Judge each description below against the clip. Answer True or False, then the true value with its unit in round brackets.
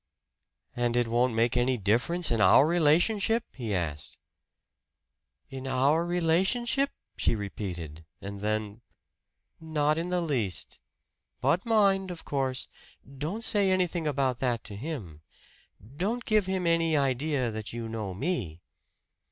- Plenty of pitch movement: True (7.7 semitones)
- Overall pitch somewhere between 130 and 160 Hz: True (135 Hz)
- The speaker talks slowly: True (130 wpm)